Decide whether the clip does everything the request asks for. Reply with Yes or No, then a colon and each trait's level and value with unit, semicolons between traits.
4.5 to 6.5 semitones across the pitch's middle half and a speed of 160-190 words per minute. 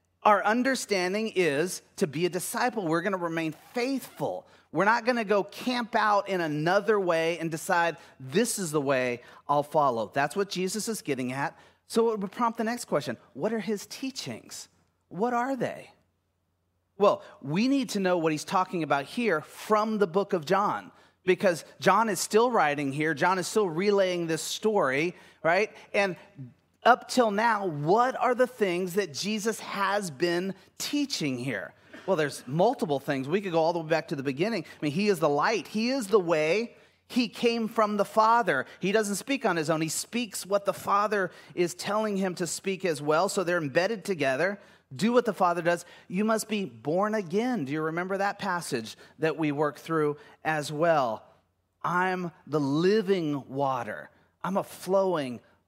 Yes: wide, 5.4 semitones; average, 185 wpm